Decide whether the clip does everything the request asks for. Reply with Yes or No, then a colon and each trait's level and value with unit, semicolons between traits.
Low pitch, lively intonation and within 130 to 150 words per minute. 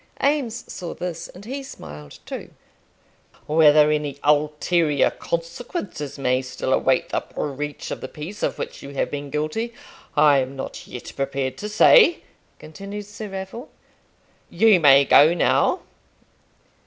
No: medium, 155 Hz; wide, 6.2 semitones; average, 140 wpm